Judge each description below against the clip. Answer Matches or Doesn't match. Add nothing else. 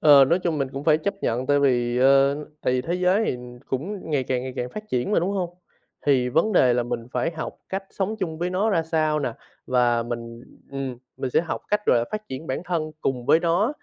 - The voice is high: Doesn't match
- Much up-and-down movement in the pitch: Matches